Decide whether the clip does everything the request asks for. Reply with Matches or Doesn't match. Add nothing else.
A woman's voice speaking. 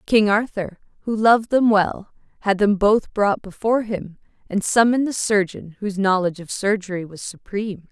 Matches